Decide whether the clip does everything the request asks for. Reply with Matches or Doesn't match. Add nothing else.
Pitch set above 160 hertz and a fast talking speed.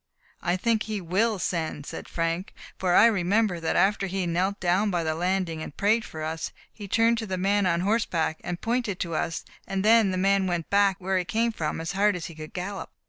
Matches